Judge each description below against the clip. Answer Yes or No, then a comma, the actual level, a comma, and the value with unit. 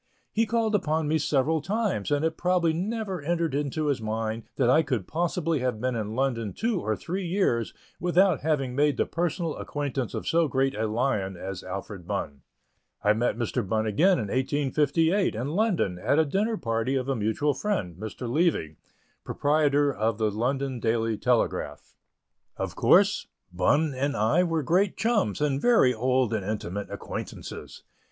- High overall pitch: No, medium, 140 Hz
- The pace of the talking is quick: No, average, 170 wpm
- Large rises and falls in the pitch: Yes, wide, 6.7 semitones